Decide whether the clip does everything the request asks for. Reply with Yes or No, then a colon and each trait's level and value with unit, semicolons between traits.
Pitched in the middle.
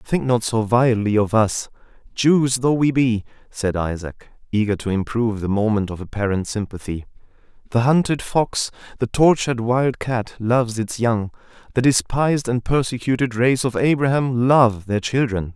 No: low, 120 Hz